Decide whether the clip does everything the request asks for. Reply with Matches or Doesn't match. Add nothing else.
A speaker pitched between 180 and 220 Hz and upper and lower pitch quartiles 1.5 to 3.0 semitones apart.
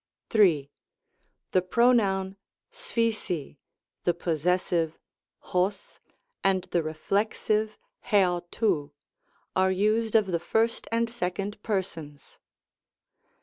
Doesn't match